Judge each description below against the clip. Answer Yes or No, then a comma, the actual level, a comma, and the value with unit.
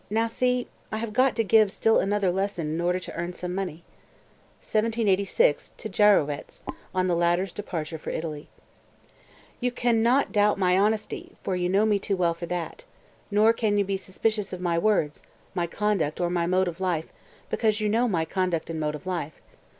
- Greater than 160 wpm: Yes, average, 195 wpm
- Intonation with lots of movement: No, average, 3.8 semitones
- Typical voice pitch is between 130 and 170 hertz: No, high, 190 Hz